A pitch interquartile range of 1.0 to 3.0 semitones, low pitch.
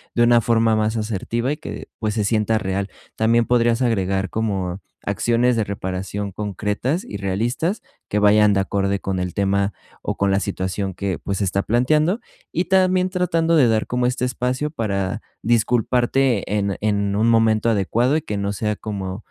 No: average, 3.5 semitones; low, 110 Hz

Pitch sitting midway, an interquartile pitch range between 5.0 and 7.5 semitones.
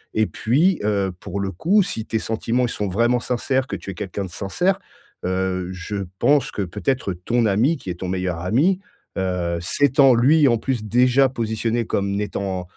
No: low, 110 Hz; average, 5.3 semitones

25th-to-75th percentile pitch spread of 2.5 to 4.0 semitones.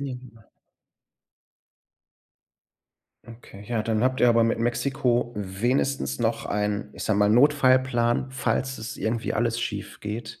Yes: average, 2.8 semitones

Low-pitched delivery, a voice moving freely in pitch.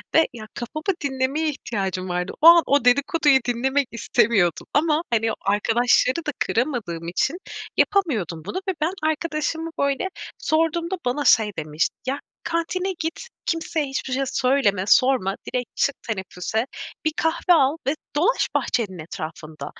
No: very high, 265 Hz; wide, 7.0 semitones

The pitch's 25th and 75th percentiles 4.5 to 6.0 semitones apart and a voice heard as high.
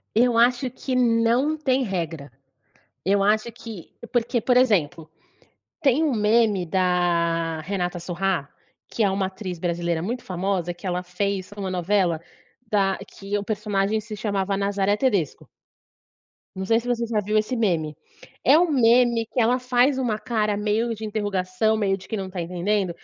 No: average, 4.1 semitones; high, 205 Hz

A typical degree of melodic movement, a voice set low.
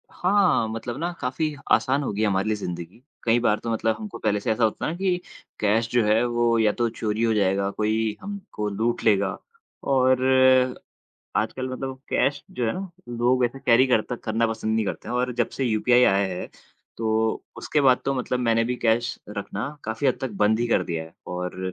Yes: average, 3.0 semitones; low, 115 Hz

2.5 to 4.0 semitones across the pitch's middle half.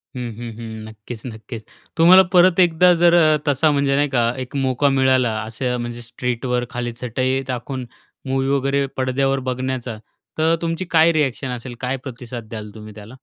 Yes: average, 2.9 semitones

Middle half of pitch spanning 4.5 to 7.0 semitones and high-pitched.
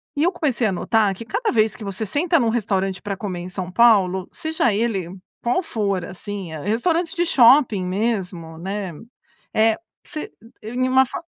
Yes: average, 5.1 semitones; high, 215 Hz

